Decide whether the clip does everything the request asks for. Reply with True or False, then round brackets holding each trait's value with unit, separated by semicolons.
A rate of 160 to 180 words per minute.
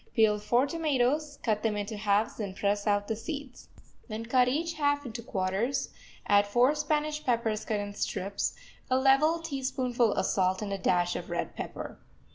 True (175 wpm)